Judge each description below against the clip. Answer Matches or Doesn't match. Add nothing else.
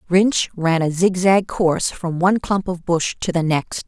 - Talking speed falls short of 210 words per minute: Matches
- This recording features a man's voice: Doesn't match